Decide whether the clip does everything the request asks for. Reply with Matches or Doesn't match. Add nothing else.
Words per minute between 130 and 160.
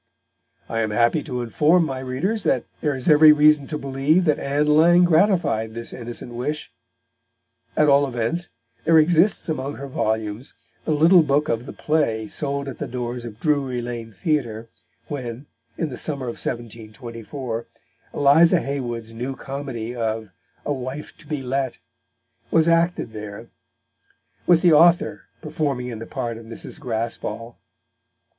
Matches